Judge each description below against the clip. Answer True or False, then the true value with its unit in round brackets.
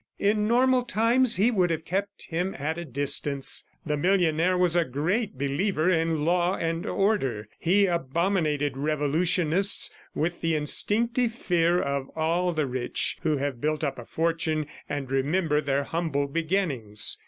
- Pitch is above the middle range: False (165 Hz)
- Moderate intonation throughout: True (4.5 semitones)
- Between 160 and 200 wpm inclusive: False (150 wpm)